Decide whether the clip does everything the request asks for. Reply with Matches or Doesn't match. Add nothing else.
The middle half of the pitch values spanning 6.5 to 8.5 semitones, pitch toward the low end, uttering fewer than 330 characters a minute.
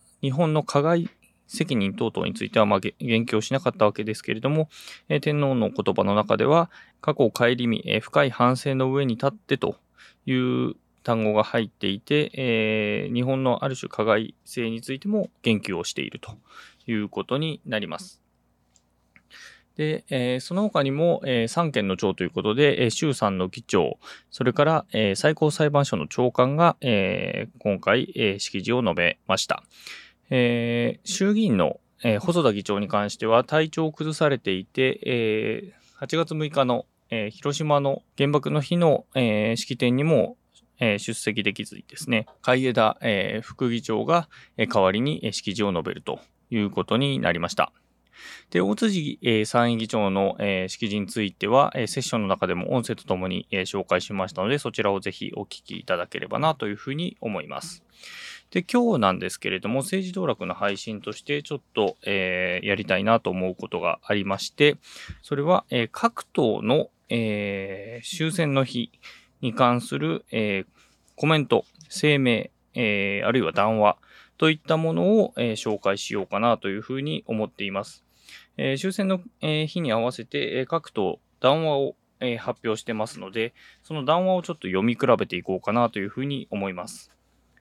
Doesn't match